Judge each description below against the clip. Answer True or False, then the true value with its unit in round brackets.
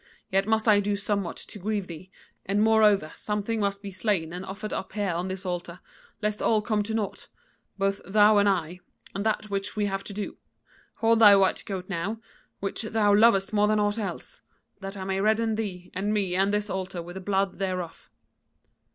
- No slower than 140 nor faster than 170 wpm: False (200 wpm)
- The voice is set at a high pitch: True (200 Hz)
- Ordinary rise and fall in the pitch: False (1.9 semitones)